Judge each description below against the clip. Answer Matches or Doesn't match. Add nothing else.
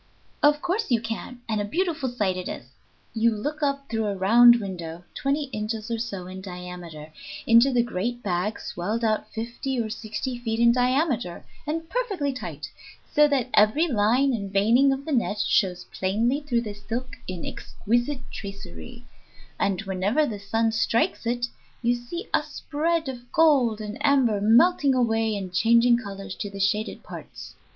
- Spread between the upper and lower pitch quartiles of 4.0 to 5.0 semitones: Matches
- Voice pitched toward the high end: Matches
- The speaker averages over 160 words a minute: Matches